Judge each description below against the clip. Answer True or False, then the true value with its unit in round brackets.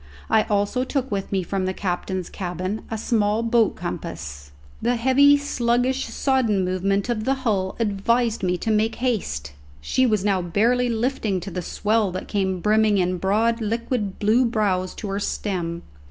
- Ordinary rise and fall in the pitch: True (3.9 semitones)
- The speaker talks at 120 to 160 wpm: False (170 wpm)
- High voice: True (210 Hz)